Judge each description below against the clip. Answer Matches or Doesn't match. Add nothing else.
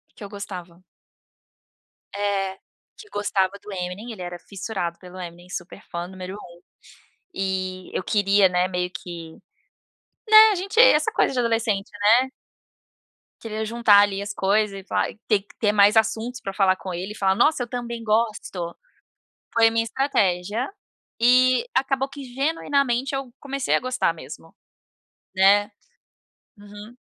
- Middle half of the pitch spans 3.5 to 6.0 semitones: Matches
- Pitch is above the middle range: Matches